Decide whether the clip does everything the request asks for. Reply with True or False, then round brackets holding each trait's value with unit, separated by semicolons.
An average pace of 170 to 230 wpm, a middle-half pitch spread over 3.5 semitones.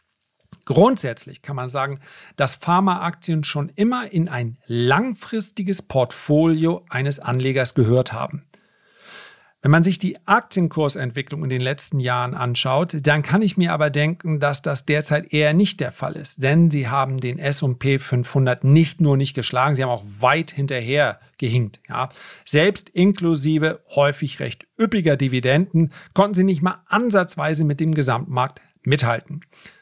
False (145 wpm; 4.0 semitones)